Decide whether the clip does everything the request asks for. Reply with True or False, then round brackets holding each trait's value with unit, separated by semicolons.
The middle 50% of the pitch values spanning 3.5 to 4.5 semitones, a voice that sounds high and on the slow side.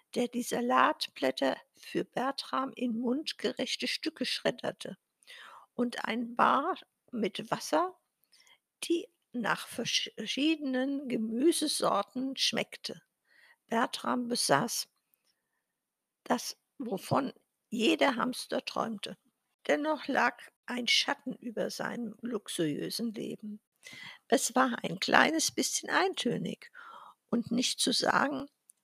True (4.2 semitones; 250 Hz; 90 wpm)